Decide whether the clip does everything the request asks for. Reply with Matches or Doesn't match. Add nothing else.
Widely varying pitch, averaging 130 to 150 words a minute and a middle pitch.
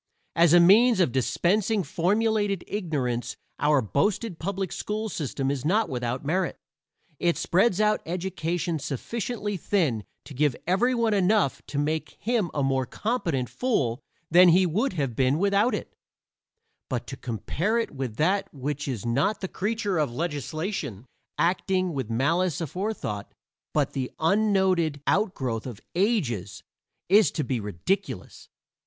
Matches